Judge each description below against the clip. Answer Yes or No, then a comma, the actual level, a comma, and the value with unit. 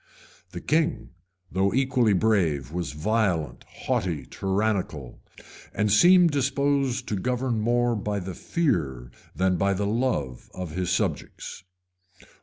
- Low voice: Yes, low, 105 Hz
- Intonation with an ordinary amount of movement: No, wide, 5.7 semitones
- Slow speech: Yes, slow, 120 wpm